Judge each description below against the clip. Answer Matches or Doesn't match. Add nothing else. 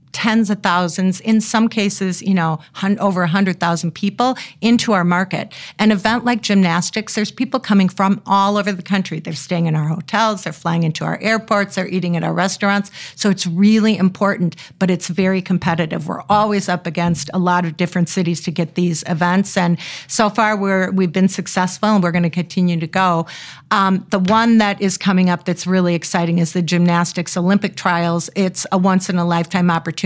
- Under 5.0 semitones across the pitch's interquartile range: Matches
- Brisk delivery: Doesn't match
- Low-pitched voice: Doesn't match